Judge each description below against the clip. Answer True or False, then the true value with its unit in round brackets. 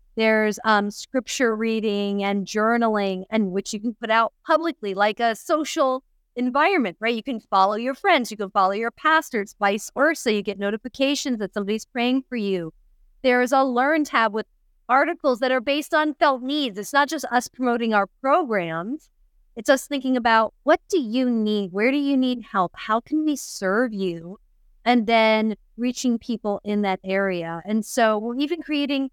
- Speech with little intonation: False (4.5 semitones)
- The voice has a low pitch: False (230 Hz)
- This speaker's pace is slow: False (180 wpm)